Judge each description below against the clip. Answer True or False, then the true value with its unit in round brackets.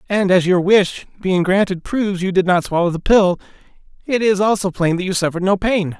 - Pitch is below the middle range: False (190 Hz)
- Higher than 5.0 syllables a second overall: True (5.6 syllables/s)